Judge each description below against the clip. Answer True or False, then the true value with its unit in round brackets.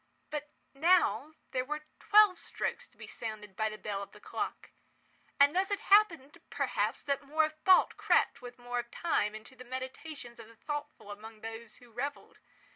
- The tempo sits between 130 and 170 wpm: False (185 wpm)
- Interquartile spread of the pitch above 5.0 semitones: True (5.5 semitones)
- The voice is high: True (260 Hz)